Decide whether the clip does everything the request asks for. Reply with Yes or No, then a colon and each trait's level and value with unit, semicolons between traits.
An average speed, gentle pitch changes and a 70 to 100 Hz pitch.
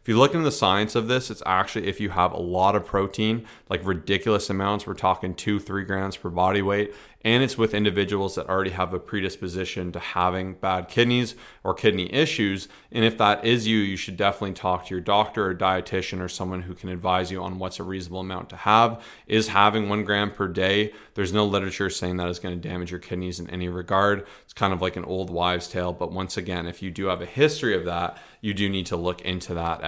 No: fast, 235 wpm; narrow, 2.2 semitones; very low, 95 Hz